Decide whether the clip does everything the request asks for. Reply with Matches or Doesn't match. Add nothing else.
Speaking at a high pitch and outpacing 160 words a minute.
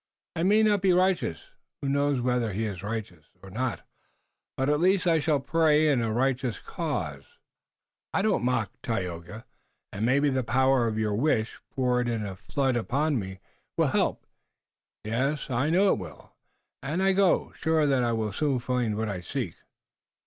Doesn't match